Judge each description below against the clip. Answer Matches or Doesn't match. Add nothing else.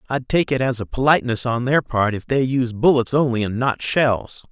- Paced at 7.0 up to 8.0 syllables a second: Doesn't match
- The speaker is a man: Matches